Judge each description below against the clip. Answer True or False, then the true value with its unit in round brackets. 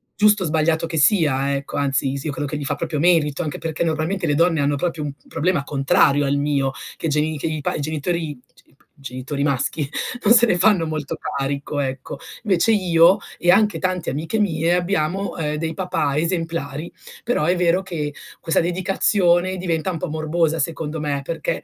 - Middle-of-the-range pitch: True (160 Hz)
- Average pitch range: True (3.4 semitones)